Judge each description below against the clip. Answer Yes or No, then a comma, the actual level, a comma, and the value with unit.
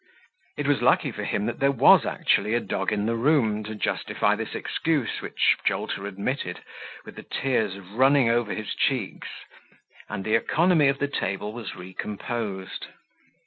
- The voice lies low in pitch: Yes, low, 115 Hz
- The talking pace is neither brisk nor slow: Yes, average, 160 wpm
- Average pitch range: Yes, average, 5.0 semitones